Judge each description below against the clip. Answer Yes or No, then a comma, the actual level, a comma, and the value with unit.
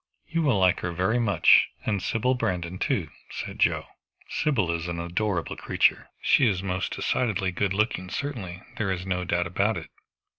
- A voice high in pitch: No, very low, 95 Hz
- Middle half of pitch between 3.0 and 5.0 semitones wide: Yes, average, 3.8 semitones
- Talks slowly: No, average, 175 wpm